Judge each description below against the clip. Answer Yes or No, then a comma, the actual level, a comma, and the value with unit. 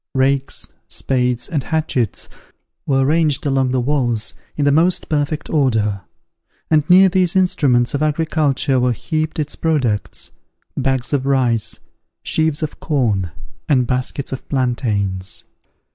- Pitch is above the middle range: No, low, 135 Hz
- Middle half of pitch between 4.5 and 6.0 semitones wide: No, average, 3.7 semitones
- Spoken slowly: Yes, slow, 130 wpm